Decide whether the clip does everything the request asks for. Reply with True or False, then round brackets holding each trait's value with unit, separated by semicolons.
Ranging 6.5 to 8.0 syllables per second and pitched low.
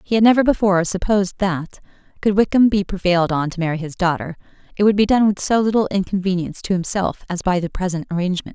False (6.6 syllables/s; 190 Hz)